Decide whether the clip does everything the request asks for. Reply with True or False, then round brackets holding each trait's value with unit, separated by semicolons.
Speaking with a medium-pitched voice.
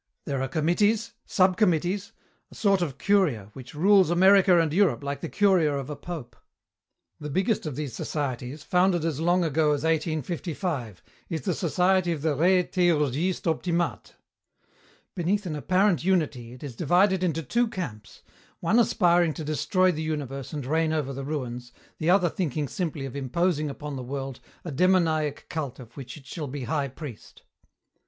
True (160 Hz)